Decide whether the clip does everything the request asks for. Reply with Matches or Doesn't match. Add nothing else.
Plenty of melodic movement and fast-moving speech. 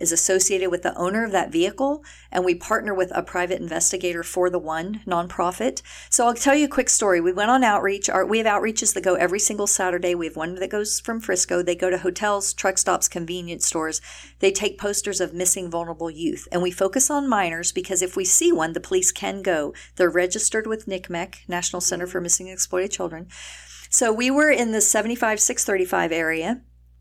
Doesn't match